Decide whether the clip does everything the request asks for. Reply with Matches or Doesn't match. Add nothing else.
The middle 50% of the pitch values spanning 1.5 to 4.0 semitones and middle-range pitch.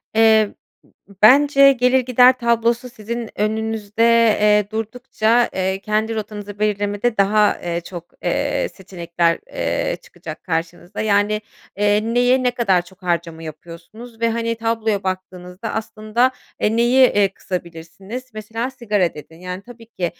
Doesn't match